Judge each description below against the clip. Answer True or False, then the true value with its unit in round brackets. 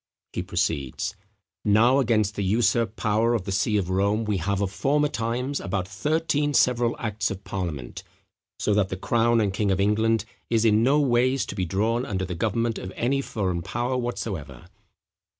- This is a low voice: True (110 Hz)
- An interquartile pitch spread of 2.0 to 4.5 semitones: True (3.6 semitones)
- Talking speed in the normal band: True (175 wpm)